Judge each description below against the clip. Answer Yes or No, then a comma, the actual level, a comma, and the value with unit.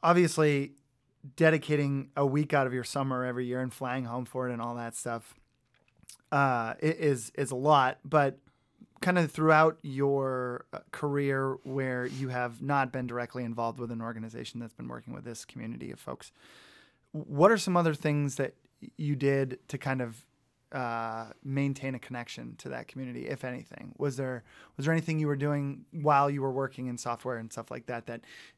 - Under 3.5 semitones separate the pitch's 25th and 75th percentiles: Yes, average, 2.8 semitones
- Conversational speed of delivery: Yes, average, 185 wpm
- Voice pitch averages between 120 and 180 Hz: Yes, low, 135 Hz